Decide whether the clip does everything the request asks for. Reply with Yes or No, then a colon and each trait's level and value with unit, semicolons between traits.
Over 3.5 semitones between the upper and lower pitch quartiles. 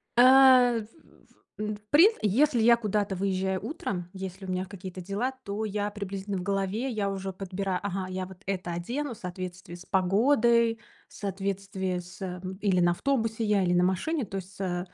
No: average, 3.0 semitones